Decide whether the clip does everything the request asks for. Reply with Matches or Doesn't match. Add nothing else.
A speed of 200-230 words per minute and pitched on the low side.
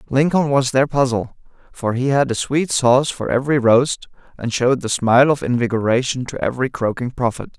Doesn't match